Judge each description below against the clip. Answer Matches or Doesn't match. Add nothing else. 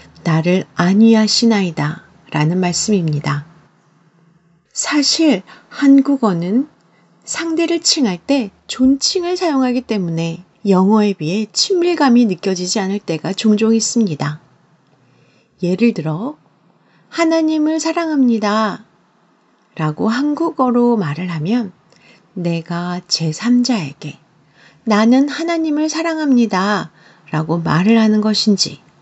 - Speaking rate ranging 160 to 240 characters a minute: Matches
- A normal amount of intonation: Doesn't match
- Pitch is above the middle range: Matches